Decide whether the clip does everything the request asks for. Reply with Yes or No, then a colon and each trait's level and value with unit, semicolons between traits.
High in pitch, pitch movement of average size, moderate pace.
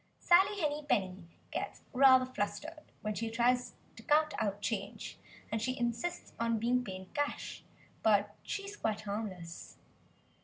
No: high, 230 Hz; wide, 6.0 semitones; average, 145 wpm